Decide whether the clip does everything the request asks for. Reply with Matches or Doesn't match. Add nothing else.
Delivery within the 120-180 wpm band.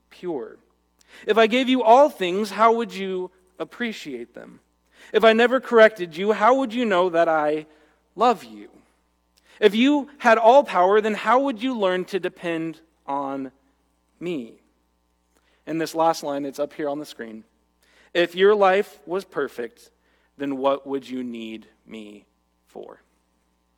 Matches